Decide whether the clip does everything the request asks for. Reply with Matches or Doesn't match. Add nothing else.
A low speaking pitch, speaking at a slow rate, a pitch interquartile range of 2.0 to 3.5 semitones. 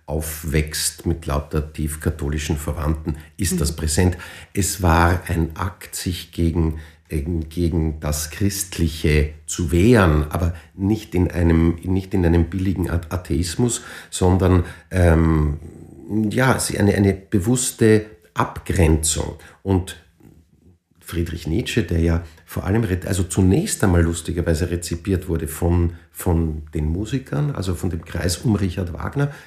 Matches